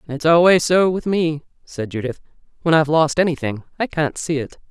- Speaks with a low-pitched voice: No, medium, 155 Hz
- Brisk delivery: No, average, 190 wpm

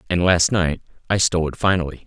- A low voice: Yes, very low, 85 Hz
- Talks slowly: No, fast, 205 wpm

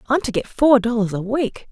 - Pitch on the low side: No, high, 235 Hz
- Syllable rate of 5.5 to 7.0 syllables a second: No, 5.3 syllables/s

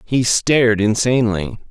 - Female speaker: No, male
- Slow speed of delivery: Yes, slow, 105 wpm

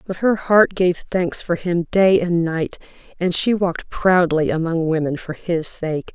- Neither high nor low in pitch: Yes, medium, 170 Hz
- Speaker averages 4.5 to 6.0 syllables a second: No, 4.1 syllables/s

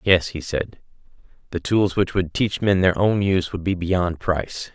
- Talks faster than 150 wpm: Yes, average, 200 wpm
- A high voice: No, very low, 90 Hz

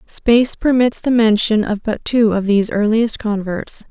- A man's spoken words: No, female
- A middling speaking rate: Yes, average, 170 wpm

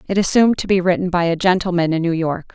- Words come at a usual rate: No, fast, 260 wpm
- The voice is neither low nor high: Yes, medium, 180 Hz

